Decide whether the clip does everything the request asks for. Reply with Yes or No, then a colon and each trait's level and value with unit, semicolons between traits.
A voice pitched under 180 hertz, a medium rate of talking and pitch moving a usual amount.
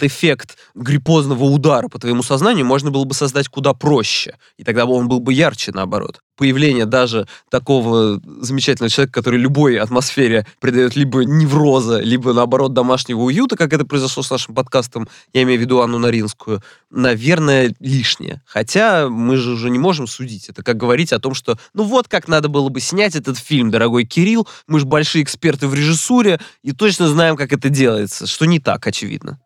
No: low, 135 Hz; fast, 180 wpm; average, 3.5 semitones